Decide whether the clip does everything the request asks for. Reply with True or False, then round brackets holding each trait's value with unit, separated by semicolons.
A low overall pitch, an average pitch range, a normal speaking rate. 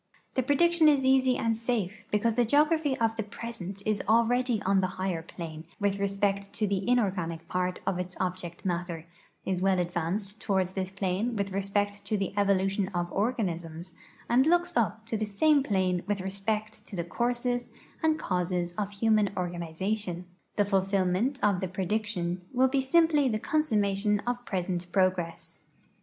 False (200 Hz; 4.0 semitones; 165 wpm)